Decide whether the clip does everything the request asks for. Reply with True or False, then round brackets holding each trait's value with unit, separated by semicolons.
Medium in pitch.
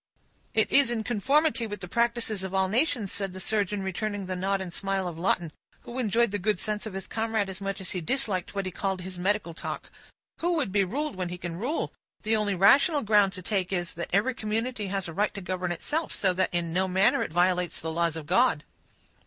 False (195 Hz)